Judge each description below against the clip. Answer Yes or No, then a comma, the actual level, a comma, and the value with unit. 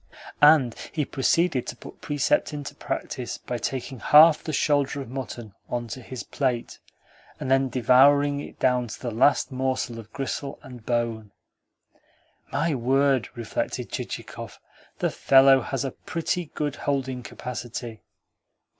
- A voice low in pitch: Yes, low, 130 Hz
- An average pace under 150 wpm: Yes, average, 140 wpm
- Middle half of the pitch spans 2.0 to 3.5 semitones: Yes, average, 2.9 semitones